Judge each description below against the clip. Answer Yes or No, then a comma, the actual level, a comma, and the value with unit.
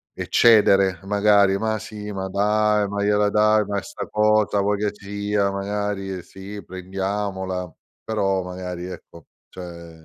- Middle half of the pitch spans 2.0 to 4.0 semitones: No, narrow, 1.6 semitones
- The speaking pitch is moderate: No, low, 100 Hz